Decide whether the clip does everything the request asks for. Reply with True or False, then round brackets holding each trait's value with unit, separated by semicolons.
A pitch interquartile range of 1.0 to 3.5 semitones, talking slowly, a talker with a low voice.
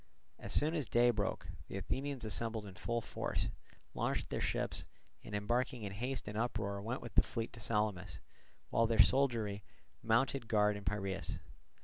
False (2.9 semitones; 165 wpm; 110 Hz)